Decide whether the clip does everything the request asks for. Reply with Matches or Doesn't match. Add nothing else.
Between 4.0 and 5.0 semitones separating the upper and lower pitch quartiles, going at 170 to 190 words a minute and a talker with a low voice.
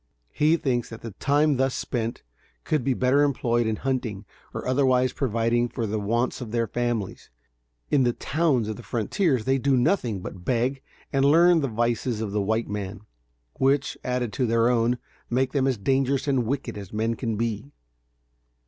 Doesn't match